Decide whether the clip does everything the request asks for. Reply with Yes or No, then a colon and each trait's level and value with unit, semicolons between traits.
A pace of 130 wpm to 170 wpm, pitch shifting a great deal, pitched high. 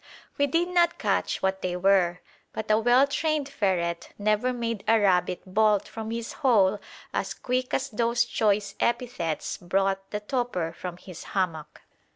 No: average, 160 wpm; average, 4.5 semitones; high, 210 Hz